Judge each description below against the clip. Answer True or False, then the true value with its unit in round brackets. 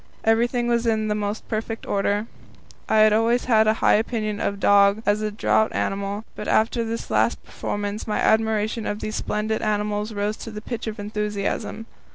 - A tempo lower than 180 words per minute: False (190 wpm)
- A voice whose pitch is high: True (215 Hz)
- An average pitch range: False (1.2 semitones)